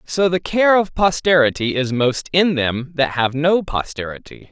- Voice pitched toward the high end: No, medium, 150 Hz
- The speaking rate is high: No, average, 175 wpm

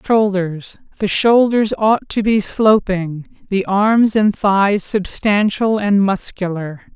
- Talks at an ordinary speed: No, slow, 110 wpm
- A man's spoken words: No, female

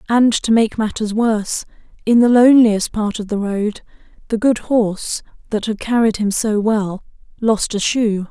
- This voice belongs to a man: No, female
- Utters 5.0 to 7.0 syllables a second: No, 4.6 syllables/s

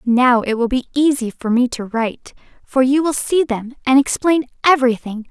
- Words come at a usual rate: Yes, average, 190 wpm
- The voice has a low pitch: No, very high, 255 Hz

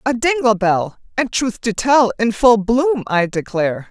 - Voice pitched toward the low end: No, high, 230 Hz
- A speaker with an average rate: Yes, average, 185 wpm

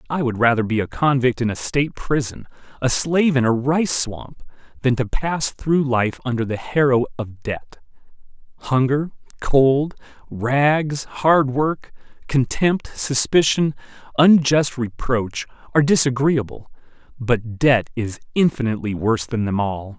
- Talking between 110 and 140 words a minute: Yes, slow, 135 wpm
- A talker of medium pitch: No, low, 130 Hz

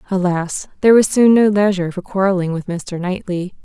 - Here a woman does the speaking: Yes, female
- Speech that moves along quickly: No, average, 180 wpm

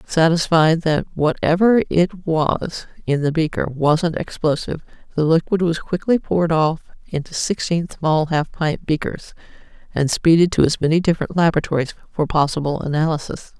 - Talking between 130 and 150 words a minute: Yes, average, 140 wpm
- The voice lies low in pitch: No, medium, 160 Hz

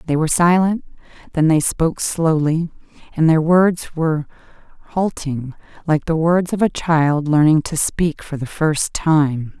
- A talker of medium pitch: Yes, medium, 160 Hz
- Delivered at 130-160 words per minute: Yes, average, 155 wpm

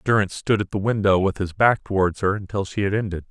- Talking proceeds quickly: Yes, fast, 255 wpm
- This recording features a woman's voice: No, male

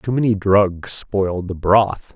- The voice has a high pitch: No, low, 100 Hz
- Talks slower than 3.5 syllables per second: Yes, 3.3 syllables/s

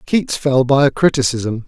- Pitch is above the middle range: No, low, 135 Hz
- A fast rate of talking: No, average, 180 wpm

